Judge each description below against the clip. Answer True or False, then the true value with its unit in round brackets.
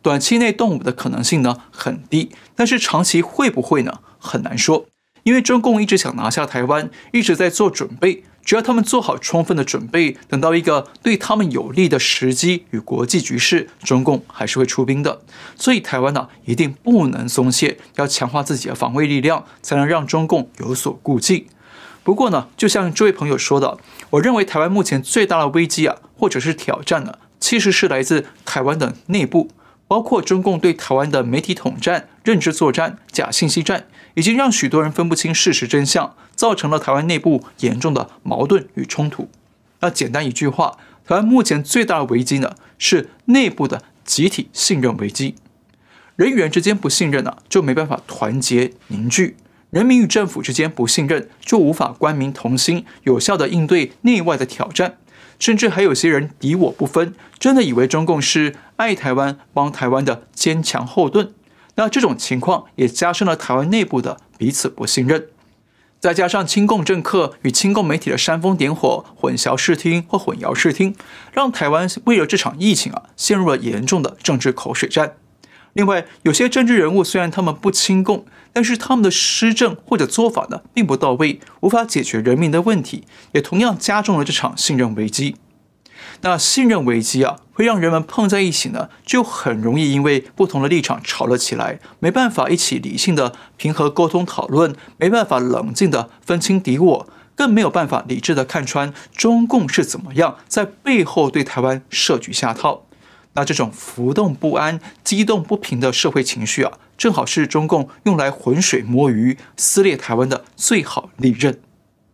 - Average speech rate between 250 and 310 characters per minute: True (285 characters per minute)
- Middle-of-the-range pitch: True (160 Hz)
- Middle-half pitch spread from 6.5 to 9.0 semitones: True (6.8 semitones)